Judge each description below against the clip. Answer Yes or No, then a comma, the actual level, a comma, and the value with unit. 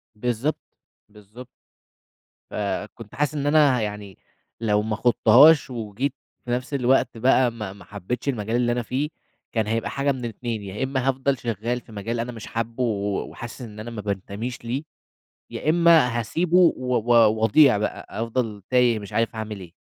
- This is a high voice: No, low, 120 Hz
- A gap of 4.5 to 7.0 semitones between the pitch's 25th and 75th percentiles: No, average, 3.3 semitones